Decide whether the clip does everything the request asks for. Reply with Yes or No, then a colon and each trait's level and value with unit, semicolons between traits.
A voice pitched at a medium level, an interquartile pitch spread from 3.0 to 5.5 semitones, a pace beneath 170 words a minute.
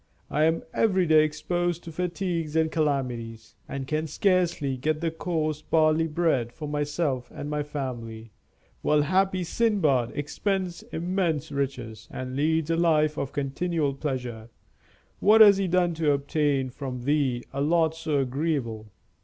Yes: medium, 155 Hz; average, 3.6 semitones; average, 145 wpm